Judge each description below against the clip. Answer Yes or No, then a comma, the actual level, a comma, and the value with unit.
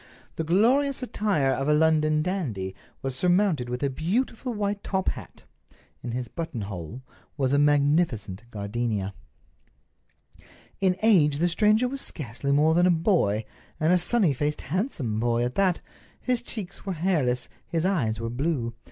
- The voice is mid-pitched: Yes, medium, 155 Hz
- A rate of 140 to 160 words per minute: Yes, average, 150 wpm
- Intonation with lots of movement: Yes, wide, 7.4 semitones